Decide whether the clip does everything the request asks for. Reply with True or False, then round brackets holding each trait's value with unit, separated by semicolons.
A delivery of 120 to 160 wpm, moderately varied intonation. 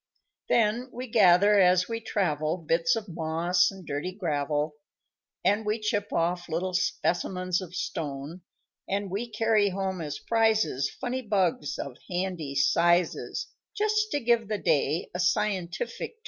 True (145 wpm; 4.2 semitones)